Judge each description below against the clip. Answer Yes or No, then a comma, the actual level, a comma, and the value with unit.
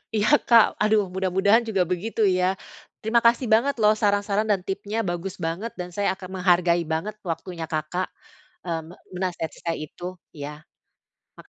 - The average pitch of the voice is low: No, high, 190 Hz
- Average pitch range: Yes, average, 3.5 semitones